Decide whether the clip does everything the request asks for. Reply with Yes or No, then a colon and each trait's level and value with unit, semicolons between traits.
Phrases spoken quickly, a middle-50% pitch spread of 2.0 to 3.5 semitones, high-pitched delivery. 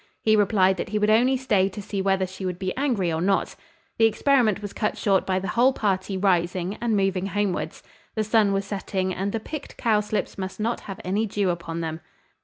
Yes: fast, 210 wpm; narrow, 2.5 semitones; high, 200 Hz